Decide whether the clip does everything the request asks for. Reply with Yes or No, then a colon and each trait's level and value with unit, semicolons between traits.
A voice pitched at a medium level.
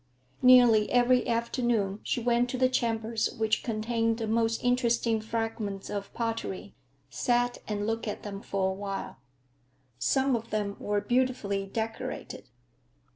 No: high, 225 Hz